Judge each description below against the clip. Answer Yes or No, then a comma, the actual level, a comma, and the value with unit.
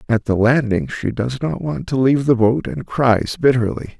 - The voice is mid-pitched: No, low, 120 Hz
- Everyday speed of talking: No, fast, 210 wpm